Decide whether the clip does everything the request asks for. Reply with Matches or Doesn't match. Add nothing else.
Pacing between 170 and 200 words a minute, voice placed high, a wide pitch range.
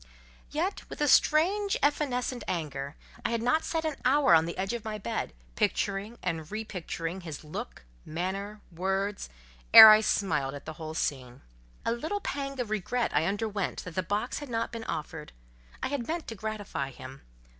Matches